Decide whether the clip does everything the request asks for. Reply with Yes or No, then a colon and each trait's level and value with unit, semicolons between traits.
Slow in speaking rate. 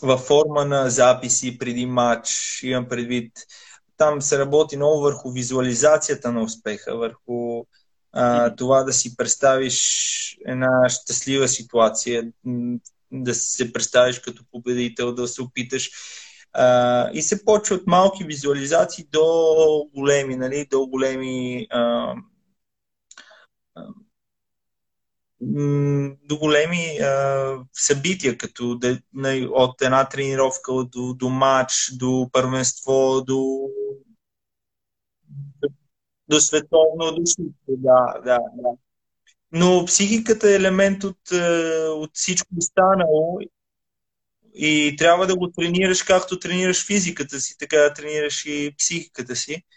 Yes: slow, 110 wpm